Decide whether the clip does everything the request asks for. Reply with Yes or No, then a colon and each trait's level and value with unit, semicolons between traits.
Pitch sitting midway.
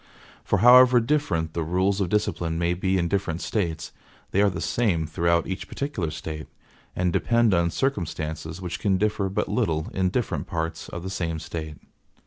No: very low, 90 Hz